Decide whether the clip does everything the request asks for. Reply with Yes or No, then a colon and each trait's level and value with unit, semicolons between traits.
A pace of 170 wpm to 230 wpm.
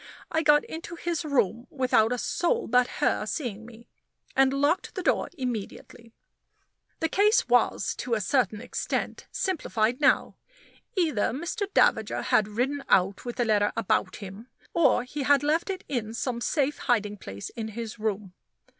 No: average, 160 wpm